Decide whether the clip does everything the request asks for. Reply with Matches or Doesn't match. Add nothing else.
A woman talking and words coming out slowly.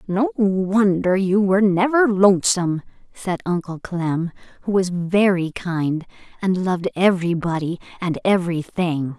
Matches